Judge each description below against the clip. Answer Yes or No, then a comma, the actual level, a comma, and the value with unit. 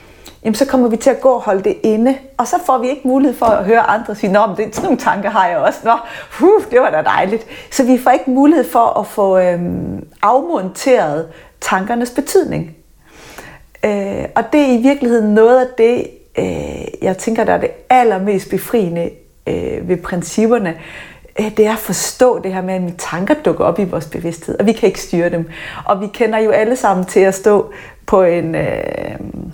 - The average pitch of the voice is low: No, high, 225 Hz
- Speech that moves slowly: No, average, 210 wpm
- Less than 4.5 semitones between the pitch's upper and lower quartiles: No, average, 5.0 semitones